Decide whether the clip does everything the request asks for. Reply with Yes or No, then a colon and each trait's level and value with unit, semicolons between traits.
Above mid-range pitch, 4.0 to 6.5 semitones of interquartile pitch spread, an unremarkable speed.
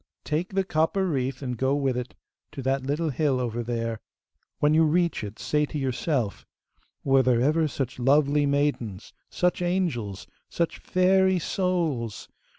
No: medium, 140 Hz; average, 4.7 semitones; average, 155 wpm